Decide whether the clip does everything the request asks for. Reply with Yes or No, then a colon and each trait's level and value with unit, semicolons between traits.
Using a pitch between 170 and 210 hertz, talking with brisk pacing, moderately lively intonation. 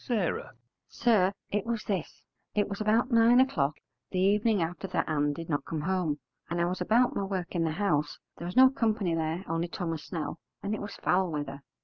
Yes: medium, 185 Hz; fast, 210 wpm; average, 4.6 semitones